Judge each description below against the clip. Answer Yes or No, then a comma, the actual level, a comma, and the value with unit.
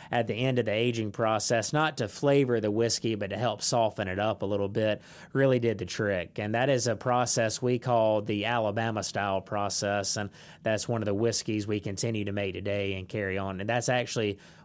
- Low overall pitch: Yes, low, 110 Hz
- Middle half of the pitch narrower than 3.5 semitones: Yes, average, 2.9 semitones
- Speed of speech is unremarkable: No, fast, 215 wpm